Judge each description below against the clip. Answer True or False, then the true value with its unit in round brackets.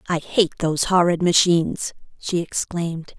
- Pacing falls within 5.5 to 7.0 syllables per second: False (4.9 syllables/s)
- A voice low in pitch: False (170 Hz)